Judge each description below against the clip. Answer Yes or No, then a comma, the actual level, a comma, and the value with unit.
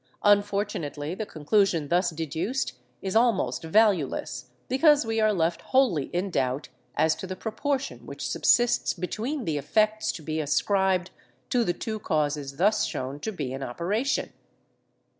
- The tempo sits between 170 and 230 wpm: No, average, 145 wpm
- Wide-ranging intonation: Yes, wide, 5.9 semitones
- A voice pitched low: No, medium, 185 Hz